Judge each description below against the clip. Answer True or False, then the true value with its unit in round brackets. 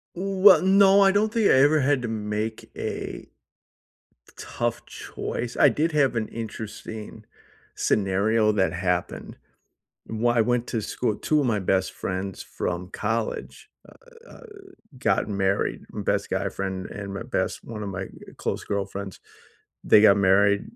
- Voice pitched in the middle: False (110 Hz)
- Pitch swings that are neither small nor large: False (6.0 semitones)